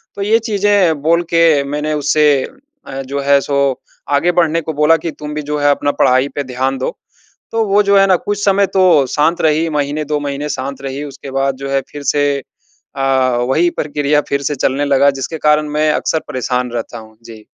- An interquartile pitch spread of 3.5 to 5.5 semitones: No, average, 2.9 semitones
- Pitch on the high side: No, medium, 150 Hz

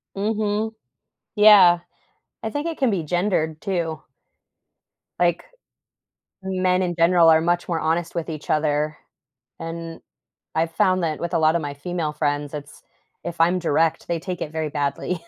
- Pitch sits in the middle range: Yes, medium, 170 Hz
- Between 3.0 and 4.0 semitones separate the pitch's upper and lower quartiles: No, narrow, 2.6 semitones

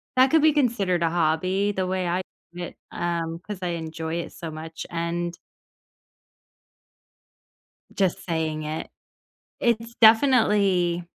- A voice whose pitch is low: No, medium, 175 Hz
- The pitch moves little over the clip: No, average, 3.7 semitones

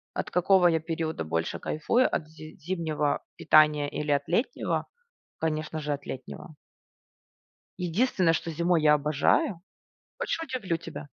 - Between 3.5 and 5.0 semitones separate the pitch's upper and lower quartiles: No, average, 2.8 semitones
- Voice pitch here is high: No, medium, 160 Hz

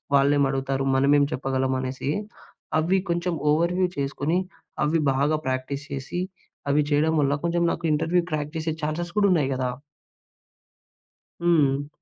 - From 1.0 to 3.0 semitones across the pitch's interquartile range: No, average, 3.6 semitones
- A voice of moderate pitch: Yes, medium, 145 Hz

